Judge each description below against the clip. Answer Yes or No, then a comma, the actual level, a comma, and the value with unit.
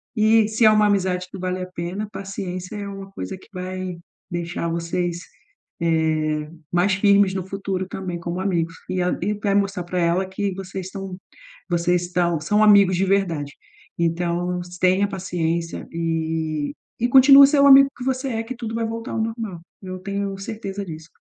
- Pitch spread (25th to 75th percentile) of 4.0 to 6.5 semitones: No, average, 2.8 semitones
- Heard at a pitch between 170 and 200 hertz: Yes, medium, 185 Hz